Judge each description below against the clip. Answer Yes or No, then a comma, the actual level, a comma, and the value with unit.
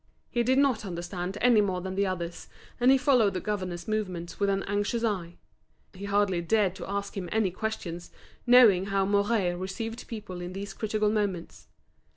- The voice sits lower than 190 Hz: No, high, 200 Hz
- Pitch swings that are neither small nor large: Yes, average, 3.0 semitones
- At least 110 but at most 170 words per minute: No, average, 180 wpm